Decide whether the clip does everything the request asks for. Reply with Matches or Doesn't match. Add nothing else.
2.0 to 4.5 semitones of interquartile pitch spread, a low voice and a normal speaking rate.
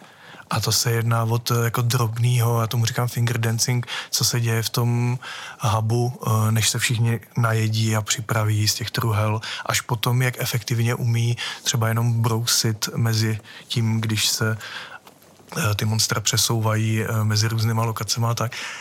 Doesn't match